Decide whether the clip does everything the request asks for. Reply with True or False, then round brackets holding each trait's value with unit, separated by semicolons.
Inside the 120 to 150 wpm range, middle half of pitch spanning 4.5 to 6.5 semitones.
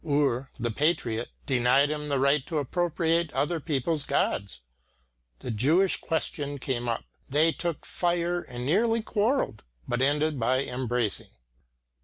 True (135 wpm; 5.0 semitones)